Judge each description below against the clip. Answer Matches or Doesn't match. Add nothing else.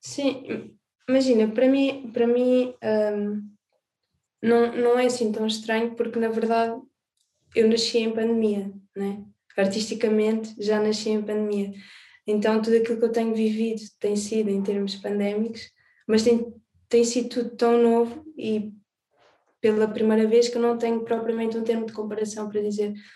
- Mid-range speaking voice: Doesn't match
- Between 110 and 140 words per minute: Doesn't match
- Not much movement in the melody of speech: Matches